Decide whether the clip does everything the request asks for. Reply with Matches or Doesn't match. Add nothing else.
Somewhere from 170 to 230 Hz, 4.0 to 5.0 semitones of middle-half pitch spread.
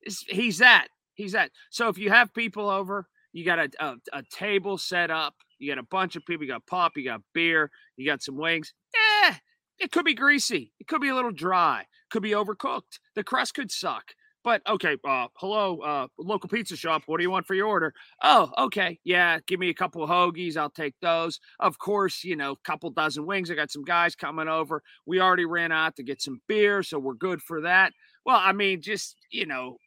Matches